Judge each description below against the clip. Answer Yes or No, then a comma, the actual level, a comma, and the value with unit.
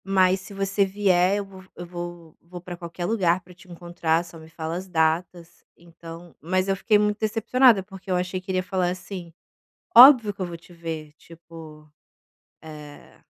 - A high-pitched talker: No, medium, 180 Hz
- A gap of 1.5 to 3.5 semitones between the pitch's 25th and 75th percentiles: Yes, narrow, 2.4 semitones